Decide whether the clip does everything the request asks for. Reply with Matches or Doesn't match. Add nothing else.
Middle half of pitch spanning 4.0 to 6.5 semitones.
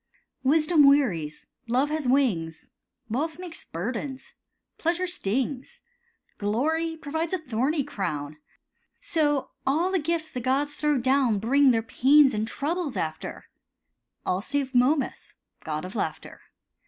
Matches